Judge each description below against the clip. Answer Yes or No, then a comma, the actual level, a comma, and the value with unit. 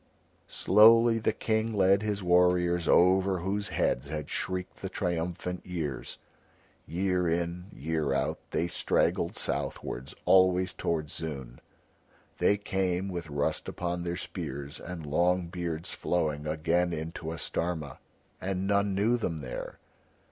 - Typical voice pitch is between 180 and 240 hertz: No, very low, 90 Hz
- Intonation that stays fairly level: No, average, 3.0 semitones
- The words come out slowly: Yes, slow, 130 wpm